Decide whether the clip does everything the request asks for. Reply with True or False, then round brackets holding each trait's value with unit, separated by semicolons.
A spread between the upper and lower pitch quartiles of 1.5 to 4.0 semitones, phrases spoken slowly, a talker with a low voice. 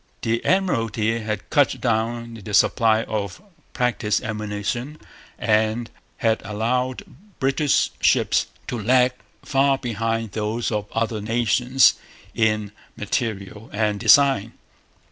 True (2.5 semitones; 105 wpm; 115 Hz)